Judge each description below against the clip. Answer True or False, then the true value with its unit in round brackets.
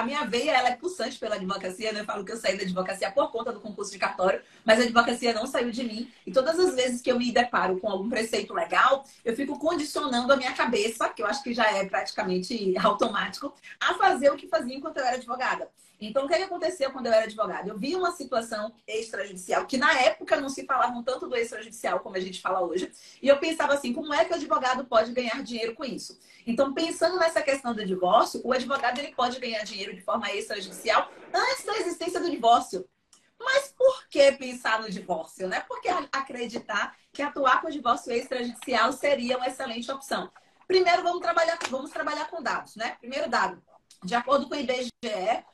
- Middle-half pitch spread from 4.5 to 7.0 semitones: True (5.1 semitones)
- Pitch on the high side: True (255 Hz)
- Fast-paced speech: True (210 wpm)